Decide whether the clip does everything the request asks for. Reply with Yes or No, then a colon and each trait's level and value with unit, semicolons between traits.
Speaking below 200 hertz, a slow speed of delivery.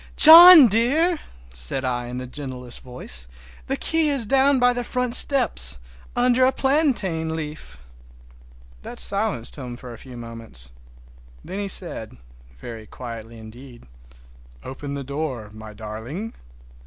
Yes: medium, 140 Hz; slow, 130 wpm